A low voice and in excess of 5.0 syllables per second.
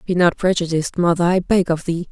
No: medium, 175 Hz; 6.1 syllables/s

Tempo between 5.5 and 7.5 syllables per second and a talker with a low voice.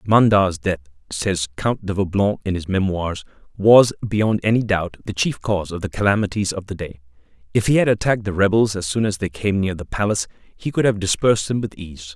Yes: 5.6 syllables/s; low, 100 Hz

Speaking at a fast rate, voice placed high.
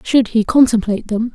No: average, 180 wpm; high, 225 Hz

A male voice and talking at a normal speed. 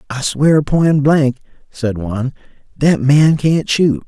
Yes: male; average, 145 wpm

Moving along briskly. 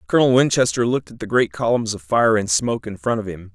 Yes: fast, 255 wpm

